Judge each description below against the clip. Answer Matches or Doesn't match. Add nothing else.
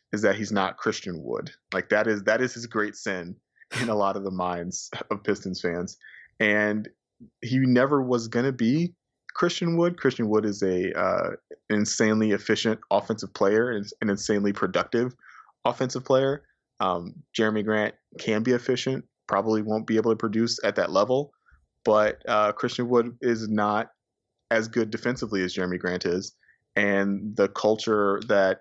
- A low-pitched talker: Matches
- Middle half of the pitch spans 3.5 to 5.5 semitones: Doesn't match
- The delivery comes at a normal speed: Matches